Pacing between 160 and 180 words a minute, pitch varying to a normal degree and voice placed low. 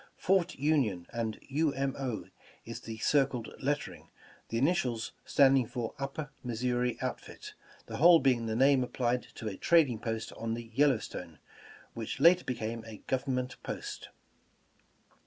No: average, 145 wpm; average, 3.5 semitones; low, 125 Hz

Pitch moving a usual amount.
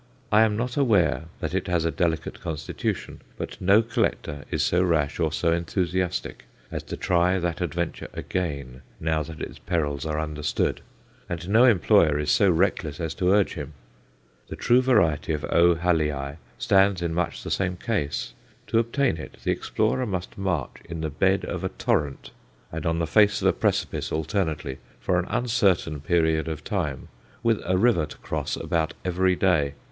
Yes: average, 3.8 semitones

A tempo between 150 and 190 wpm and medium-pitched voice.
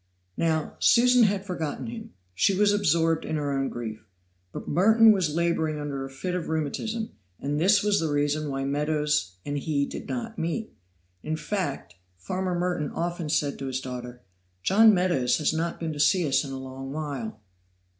Yes: average, 175 wpm; medium, 155 Hz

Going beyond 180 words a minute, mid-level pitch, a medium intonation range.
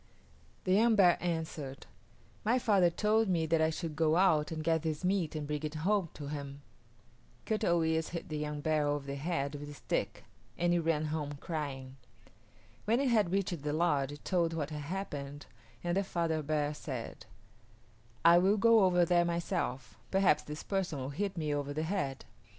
Yes: average, 190 wpm; medium, 160 Hz; average, 3.7 semitones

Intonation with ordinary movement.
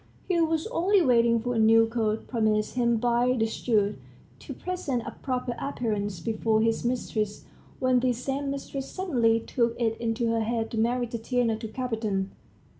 No: narrow, 2.2 semitones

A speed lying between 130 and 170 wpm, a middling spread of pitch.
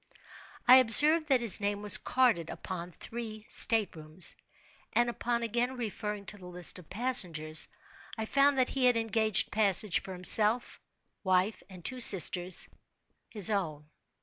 Yes: average, 145 wpm; average, 4.7 semitones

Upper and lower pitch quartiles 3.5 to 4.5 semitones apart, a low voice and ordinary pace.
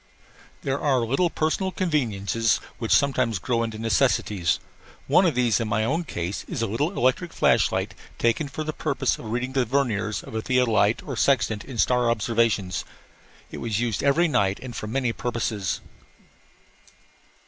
Yes: average, 3.9 semitones; low, 120 Hz; average, 165 wpm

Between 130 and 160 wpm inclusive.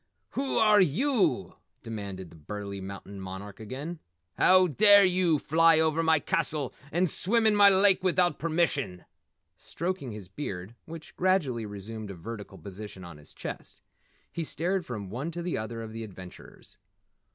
Yes: average, 155 wpm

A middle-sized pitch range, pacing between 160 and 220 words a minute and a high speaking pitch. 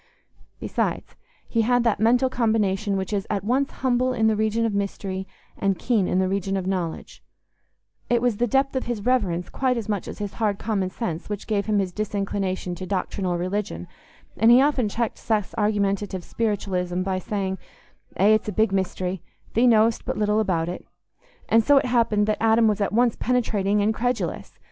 Yes: average, 3.1 semitones; average, 190 wpm; high, 210 Hz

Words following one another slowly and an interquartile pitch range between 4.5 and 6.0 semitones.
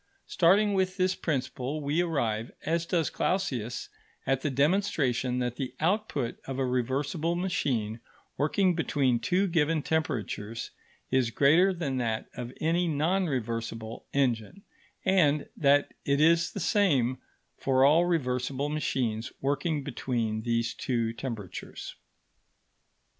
Yes: slow, 125 wpm; average, 5.3 semitones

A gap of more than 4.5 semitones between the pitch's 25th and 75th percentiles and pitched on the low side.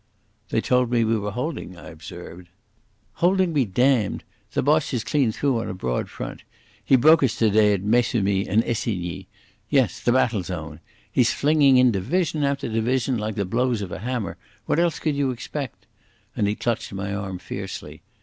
Yes: average, 5.2 semitones; low, 115 Hz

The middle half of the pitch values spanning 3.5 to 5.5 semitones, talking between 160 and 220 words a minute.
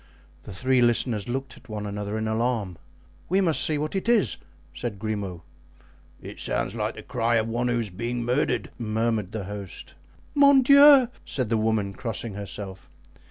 Yes: average, 3.9 semitones; average, 170 wpm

